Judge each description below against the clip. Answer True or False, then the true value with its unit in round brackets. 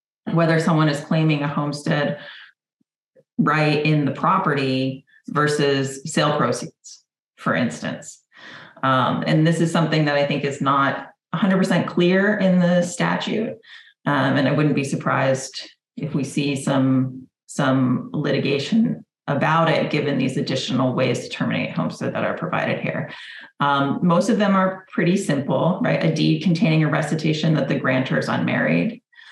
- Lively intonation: False (3.9 semitones)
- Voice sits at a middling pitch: True (150 Hz)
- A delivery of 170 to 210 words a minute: False (150 wpm)